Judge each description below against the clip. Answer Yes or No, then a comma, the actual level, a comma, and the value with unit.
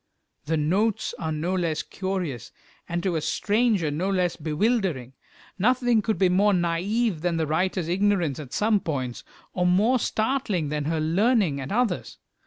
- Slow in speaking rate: No, average, 160 wpm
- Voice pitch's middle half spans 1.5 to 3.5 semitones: No, average, 4.9 semitones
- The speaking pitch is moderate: Yes, medium, 180 Hz